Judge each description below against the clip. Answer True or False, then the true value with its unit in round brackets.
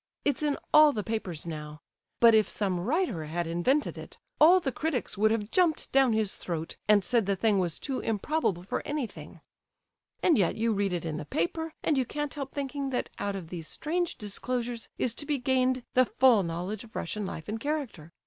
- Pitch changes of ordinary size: False (7.2 semitones)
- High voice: True (225 Hz)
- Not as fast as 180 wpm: False (205 wpm)